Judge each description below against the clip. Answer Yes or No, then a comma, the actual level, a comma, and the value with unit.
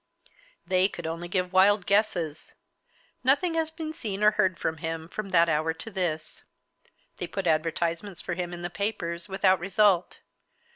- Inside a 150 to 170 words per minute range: Yes, average, 160 wpm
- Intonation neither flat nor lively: Yes, average, 3.4 semitones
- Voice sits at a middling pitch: Yes, medium, 180 Hz